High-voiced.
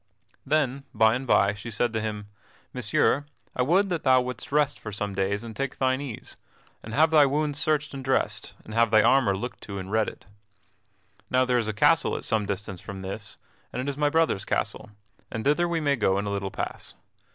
No: low, 120 Hz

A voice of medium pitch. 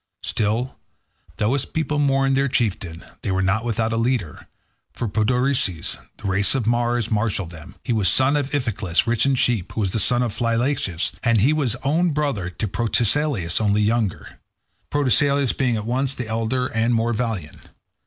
No: low, 115 Hz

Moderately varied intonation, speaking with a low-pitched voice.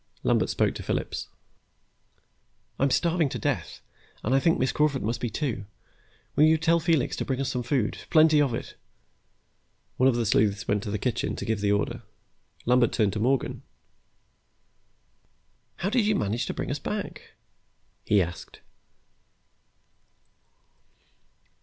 No: wide, 6.0 semitones; low, 130 Hz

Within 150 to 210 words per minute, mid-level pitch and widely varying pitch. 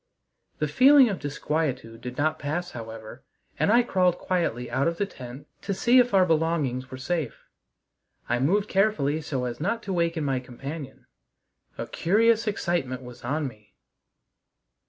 Yes: average, 155 wpm; medium, 155 Hz; wide, 6.6 semitones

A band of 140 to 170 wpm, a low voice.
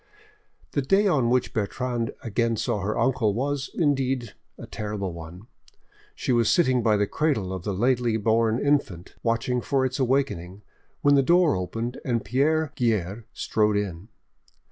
Yes: average, 155 wpm; low, 120 Hz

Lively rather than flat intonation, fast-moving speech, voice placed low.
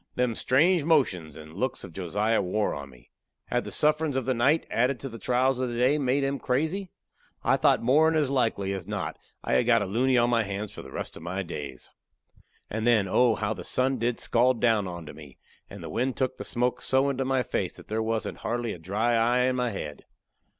No: average, 4.6 semitones; fast, 225 wpm; low, 120 Hz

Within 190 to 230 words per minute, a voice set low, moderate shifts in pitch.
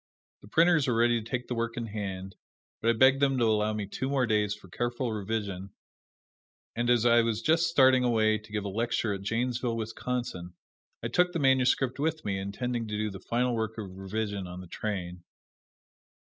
Yes: average, 200 wpm; low, 115 Hz; average, 3.4 semitones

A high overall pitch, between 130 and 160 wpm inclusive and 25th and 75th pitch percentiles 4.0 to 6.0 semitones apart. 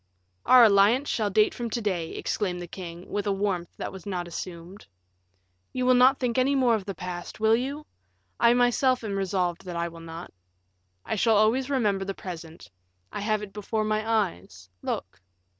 No: high, 205 Hz; average, 190 wpm; average, 4.8 semitones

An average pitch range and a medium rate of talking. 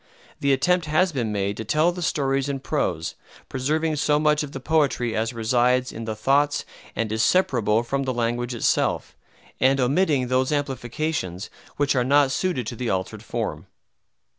Yes: average, 4.1 semitones; average, 170 wpm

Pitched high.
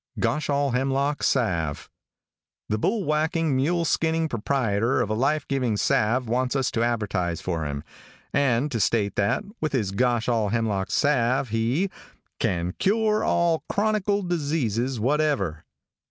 No: low, 130 Hz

